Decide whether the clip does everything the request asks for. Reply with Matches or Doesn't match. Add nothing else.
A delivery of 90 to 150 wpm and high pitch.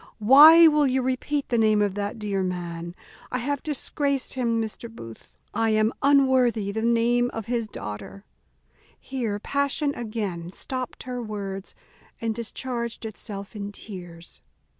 Matches